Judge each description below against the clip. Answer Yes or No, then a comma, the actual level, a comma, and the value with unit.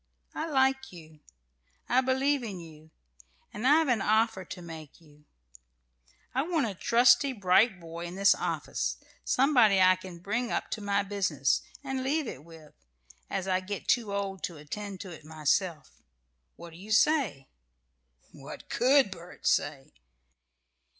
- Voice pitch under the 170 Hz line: No, high, 200 Hz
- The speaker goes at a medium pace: Yes, average, 155 wpm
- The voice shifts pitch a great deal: Yes, wide, 6.7 semitones